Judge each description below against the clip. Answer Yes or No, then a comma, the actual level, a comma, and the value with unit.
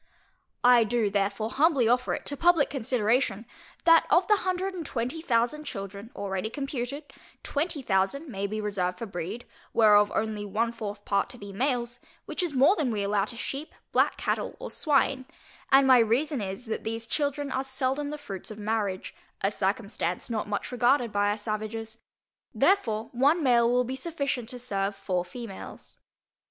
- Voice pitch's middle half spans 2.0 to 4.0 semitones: No, average, 4.9 semitones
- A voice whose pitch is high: Yes, high, 235 Hz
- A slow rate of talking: No, average, 175 wpm